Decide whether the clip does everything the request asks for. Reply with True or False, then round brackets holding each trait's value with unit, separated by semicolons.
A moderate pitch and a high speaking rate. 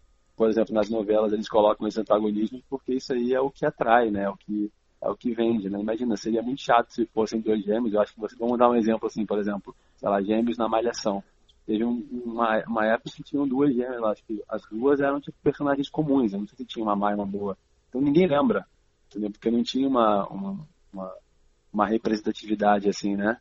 False (110 Hz; 220 wpm)